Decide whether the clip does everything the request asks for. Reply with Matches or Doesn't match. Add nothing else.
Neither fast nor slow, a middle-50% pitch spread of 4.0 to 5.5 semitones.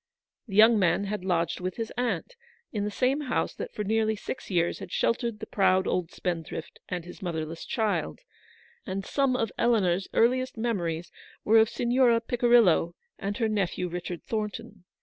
Matches